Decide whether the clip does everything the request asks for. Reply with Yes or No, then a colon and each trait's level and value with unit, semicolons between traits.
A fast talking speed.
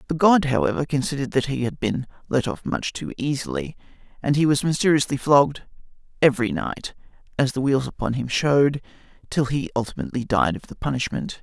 No: average, 175 wpm